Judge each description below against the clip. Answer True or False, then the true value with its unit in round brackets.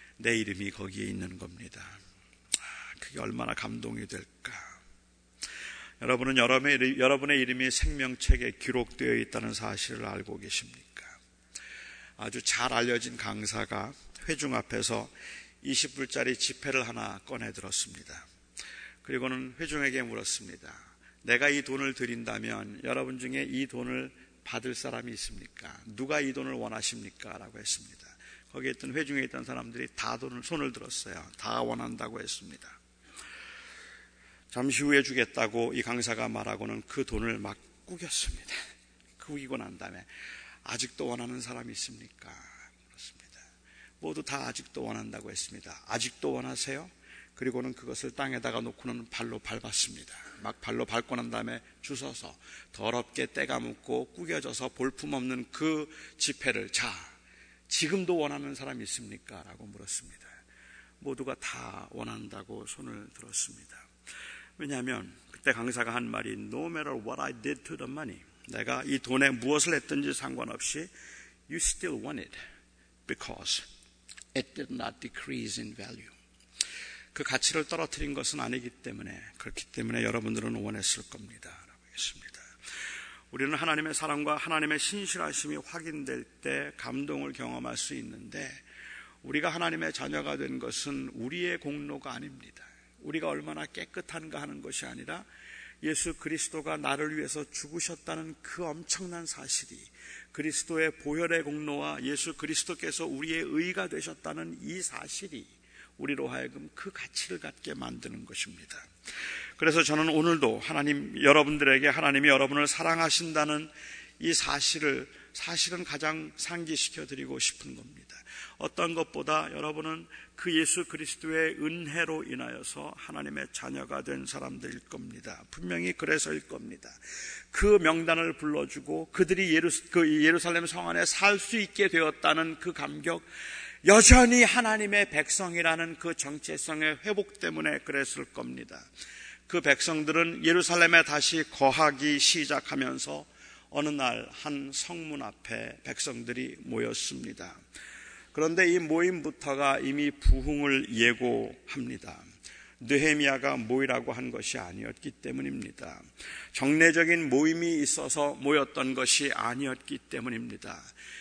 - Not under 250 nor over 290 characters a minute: False (325 characters per minute)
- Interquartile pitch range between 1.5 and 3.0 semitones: False (5.4 semitones)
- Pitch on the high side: False (140 Hz)